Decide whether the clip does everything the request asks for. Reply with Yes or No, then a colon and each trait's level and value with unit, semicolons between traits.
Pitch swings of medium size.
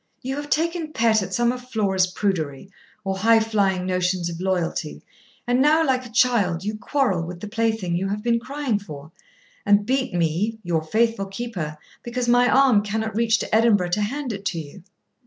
Yes: average, 4.7 semitones